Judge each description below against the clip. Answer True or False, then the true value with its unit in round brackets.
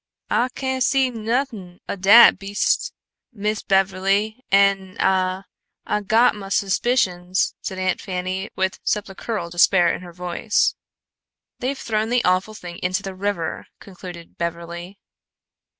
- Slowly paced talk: True (130 wpm)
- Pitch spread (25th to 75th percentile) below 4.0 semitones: True (2.9 semitones)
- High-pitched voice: True (195 Hz)